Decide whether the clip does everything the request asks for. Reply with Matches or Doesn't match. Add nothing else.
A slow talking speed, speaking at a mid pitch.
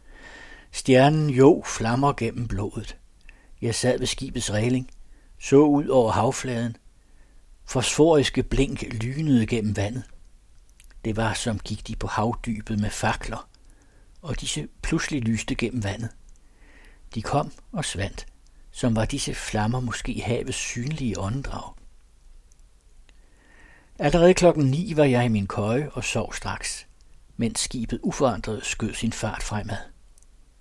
Doesn't match